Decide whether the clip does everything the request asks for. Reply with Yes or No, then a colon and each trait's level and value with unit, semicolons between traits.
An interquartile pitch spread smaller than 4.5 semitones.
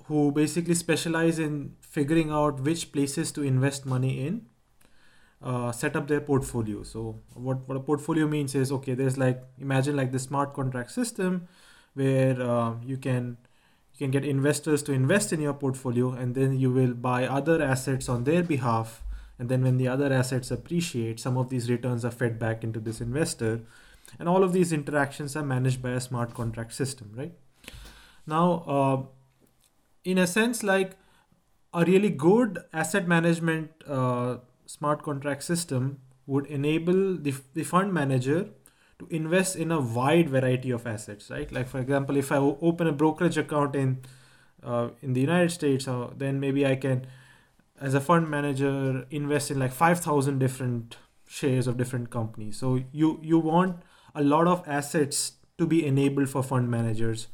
Yes: average, 3.7 semitones